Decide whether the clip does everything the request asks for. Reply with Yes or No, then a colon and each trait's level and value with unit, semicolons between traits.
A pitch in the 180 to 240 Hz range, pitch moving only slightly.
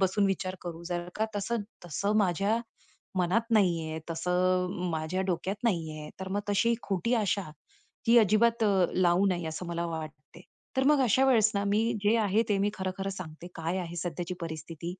No: medium, 185 Hz; average, 3.2 semitones